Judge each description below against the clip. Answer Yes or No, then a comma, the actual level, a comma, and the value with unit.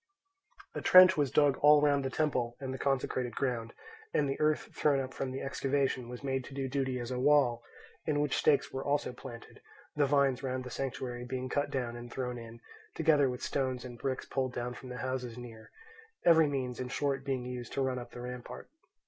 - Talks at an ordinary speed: No, fast, 210 wpm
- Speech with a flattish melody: Yes, narrow, 2.1 semitones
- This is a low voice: Yes, low, 130 Hz